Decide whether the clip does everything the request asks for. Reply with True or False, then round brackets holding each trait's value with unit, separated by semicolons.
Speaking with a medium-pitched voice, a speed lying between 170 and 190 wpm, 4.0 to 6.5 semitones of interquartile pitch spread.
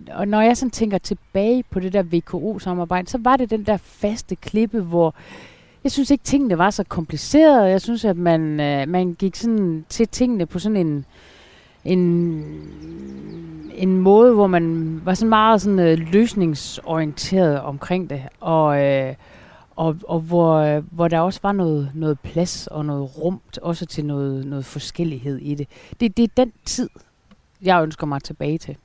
True (175 Hz; 180 wpm; 4.9 semitones)